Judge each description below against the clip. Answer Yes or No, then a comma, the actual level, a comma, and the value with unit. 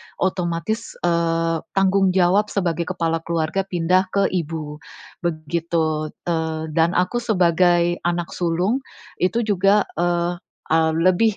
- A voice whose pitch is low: No, medium, 175 Hz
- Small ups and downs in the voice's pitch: Yes, narrow, 2.2 semitones